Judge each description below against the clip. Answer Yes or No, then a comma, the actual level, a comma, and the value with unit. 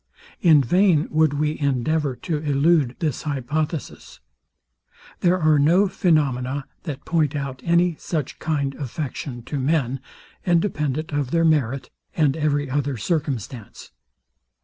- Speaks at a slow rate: Yes, slow, 125 wpm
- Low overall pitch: No, medium, 150 Hz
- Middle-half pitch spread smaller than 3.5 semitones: Yes, average, 2.8 semitones